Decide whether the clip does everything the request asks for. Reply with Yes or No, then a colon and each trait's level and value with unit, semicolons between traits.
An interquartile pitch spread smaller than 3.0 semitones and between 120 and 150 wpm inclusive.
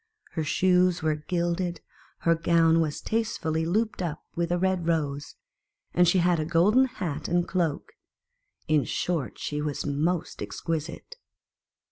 Yes: narrow, 2.4 semitones; average, 145 wpm